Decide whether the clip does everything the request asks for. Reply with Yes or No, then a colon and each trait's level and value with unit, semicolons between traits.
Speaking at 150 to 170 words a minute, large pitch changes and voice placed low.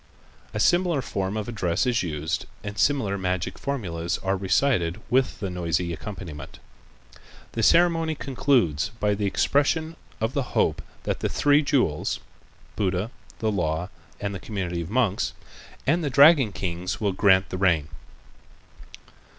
No: average, 140 wpm; wide, 6.9 semitones; low, 100 Hz